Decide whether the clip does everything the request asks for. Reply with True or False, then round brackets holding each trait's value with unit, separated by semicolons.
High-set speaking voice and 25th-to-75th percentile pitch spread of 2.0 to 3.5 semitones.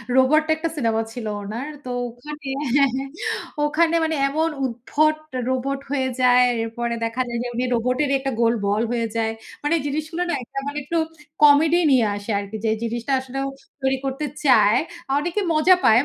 False (265 Hz; 4.2 semitones)